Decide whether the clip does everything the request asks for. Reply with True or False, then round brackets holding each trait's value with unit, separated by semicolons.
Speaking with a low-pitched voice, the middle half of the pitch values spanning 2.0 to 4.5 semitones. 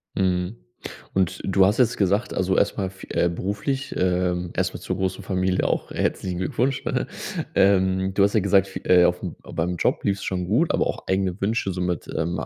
False (95 Hz; 1.6 semitones)